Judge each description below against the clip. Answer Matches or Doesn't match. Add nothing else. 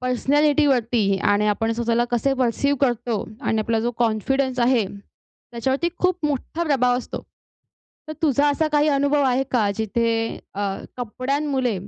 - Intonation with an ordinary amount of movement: Matches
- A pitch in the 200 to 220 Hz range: Doesn't match